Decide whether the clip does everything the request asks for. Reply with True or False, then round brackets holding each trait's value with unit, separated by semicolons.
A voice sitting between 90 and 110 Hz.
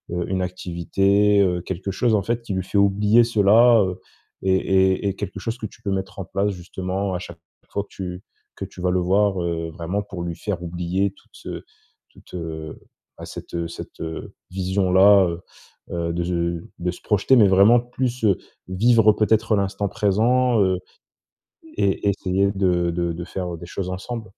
True (95 Hz)